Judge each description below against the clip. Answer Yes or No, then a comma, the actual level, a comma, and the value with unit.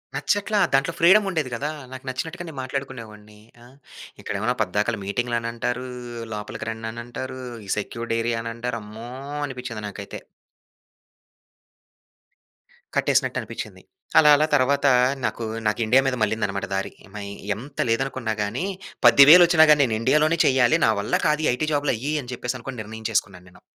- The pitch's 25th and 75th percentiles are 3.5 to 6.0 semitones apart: Yes, average, 4.0 semitones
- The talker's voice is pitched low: Yes, low, 120 Hz